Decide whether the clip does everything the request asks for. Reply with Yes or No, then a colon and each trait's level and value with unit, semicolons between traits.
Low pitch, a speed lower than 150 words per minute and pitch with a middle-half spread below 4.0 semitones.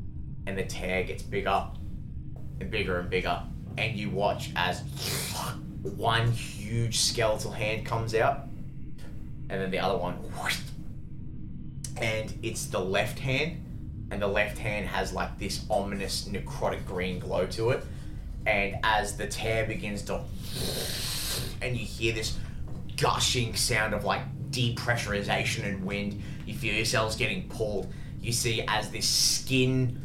Yes: low, 110 Hz; average, 140 wpm; average, 3.5 semitones